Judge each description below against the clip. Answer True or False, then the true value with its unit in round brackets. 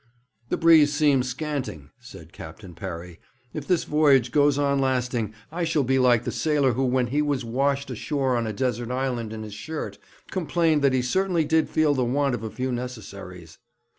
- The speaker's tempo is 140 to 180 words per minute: False (190 wpm)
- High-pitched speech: False (130 Hz)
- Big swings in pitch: False (3.8 semitones)